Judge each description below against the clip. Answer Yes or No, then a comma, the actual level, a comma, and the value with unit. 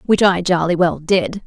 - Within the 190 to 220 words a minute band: Yes, fast, 205 wpm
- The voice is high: No, medium, 180 Hz